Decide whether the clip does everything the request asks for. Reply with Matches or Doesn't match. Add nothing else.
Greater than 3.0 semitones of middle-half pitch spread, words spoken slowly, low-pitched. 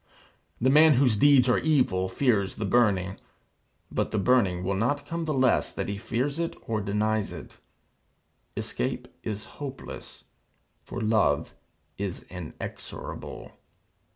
Matches